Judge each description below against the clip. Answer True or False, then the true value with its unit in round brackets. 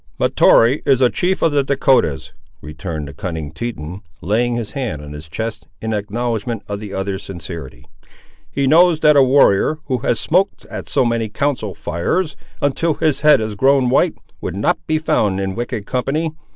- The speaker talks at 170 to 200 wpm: True (180 wpm)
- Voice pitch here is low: True (115 Hz)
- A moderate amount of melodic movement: False (6.4 semitones)